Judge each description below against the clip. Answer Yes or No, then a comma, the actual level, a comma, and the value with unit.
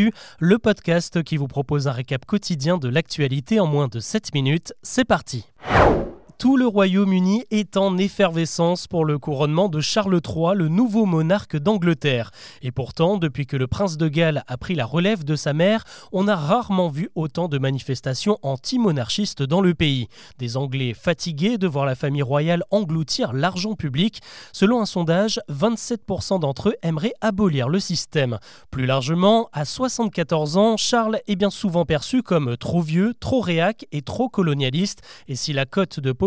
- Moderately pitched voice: Yes, medium, 170 Hz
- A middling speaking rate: Yes, average, 170 wpm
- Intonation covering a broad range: Yes, wide, 6.0 semitones